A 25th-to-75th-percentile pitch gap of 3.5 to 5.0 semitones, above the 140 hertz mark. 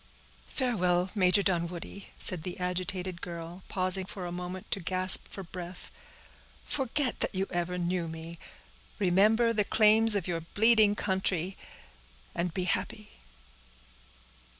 No: narrow, 2.5 semitones; medium, 185 Hz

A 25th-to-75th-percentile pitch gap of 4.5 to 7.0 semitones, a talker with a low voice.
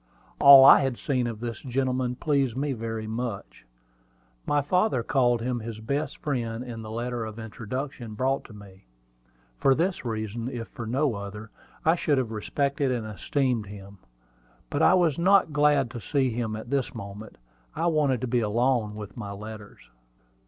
No: average, 3.8 semitones; low, 120 Hz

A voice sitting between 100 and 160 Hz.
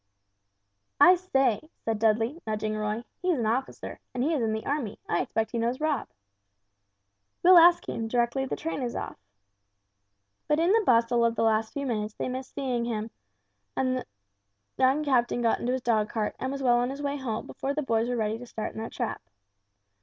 No: high, 245 Hz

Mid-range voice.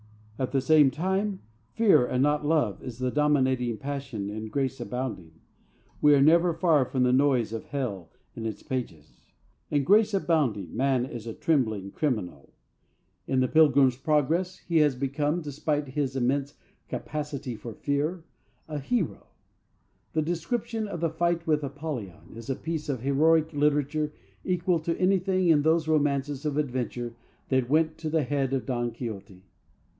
Yes: medium, 145 Hz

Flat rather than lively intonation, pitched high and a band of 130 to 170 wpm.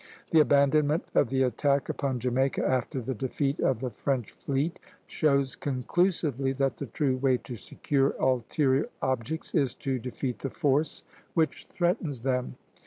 No: narrow, 2.2 semitones; low, 135 Hz; average, 150 wpm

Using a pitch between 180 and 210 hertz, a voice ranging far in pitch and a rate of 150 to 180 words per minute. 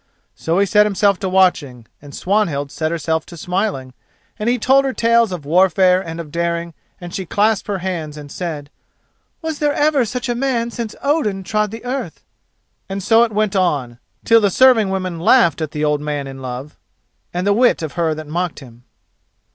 No: medium, 185 Hz; wide, 5.9 semitones; average, 195 wpm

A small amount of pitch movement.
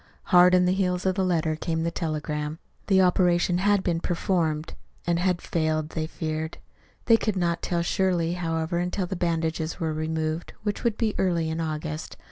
Yes: narrow, 2.3 semitones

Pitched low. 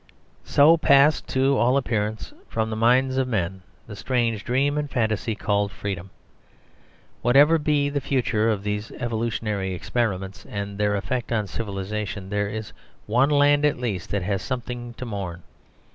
Yes: low, 110 Hz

